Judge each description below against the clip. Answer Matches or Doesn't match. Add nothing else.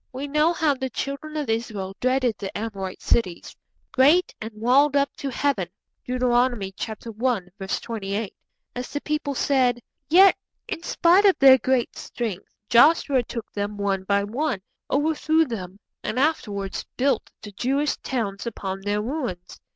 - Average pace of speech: Matches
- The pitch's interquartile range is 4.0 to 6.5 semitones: Matches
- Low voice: Doesn't match